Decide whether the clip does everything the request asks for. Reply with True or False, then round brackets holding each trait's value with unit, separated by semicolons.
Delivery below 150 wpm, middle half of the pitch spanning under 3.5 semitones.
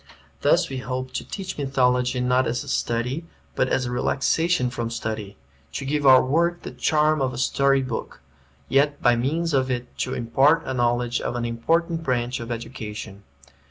False (180 wpm; 2.9 semitones)